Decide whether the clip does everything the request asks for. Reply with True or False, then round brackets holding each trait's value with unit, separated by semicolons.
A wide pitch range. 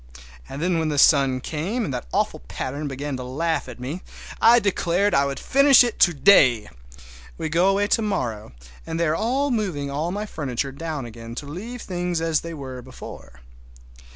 True (6.2 semitones)